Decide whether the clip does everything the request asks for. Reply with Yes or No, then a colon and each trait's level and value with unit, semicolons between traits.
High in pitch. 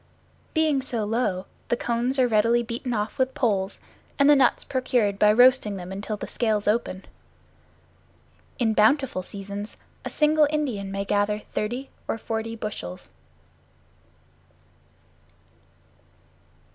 Yes: high, 225 Hz